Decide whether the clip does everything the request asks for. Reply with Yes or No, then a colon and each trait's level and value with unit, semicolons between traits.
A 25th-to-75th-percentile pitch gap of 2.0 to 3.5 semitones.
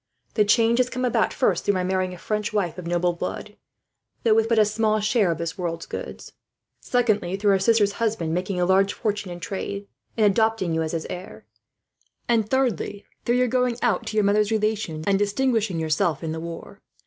No: average, 3.9 semitones